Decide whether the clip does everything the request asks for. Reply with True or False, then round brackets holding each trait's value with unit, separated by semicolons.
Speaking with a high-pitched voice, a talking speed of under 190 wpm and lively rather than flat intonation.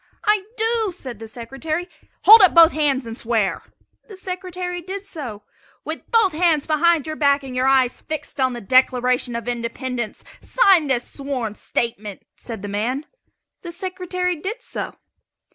True (285 Hz; 160 wpm; 6.9 semitones)